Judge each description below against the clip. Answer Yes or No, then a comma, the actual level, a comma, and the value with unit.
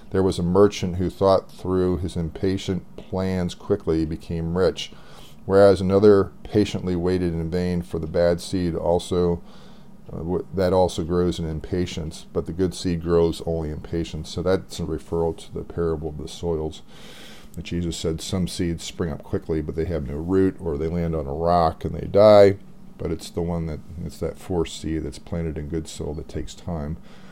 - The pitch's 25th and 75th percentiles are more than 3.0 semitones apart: No, narrow, 2.5 semitones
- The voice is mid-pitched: No, very low, 85 Hz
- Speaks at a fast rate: No, average, 195 wpm